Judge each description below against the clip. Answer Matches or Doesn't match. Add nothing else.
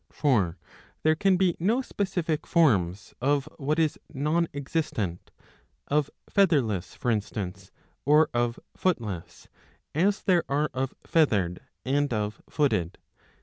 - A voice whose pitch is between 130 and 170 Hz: Matches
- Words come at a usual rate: Doesn't match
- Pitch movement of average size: Doesn't match